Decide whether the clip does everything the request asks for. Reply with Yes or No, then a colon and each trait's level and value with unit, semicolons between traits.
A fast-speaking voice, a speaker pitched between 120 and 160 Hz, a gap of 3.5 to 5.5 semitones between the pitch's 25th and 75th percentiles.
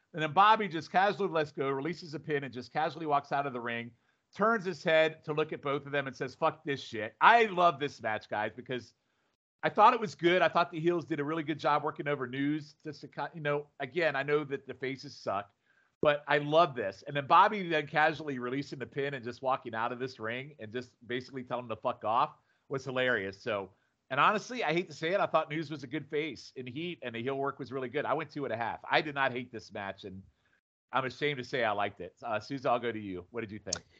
Yes: fast, 265 wpm; medium, 140 Hz; average, 4.2 semitones